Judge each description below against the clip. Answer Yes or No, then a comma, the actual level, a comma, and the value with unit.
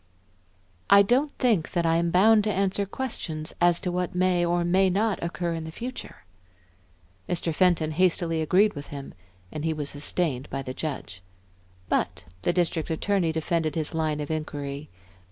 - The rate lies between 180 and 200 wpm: No, average, 170 wpm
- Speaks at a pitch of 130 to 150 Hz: No, medium, 170 Hz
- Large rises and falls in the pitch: No, average, 3.2 semitones